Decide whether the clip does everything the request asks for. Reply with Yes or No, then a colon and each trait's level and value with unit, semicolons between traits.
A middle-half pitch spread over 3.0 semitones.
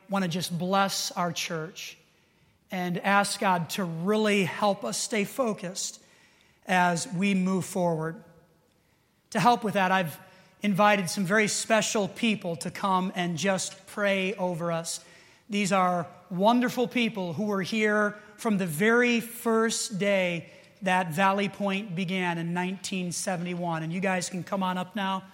No: narrow, 2.5 semitones